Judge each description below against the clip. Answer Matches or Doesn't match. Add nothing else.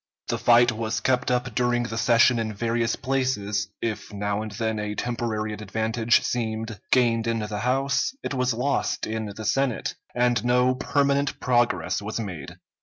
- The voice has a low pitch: Matches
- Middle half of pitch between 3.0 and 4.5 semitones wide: Doesn't match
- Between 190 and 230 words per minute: Doesn't match